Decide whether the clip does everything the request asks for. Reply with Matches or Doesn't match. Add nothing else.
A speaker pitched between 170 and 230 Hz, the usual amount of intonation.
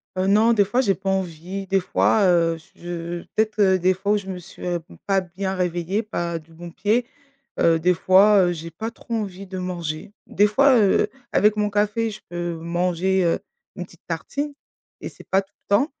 Matches